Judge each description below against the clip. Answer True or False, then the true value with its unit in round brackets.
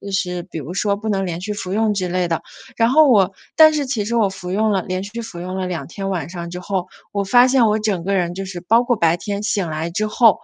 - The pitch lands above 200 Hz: False (195 Hz)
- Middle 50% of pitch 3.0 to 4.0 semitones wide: True (3.4 semitones)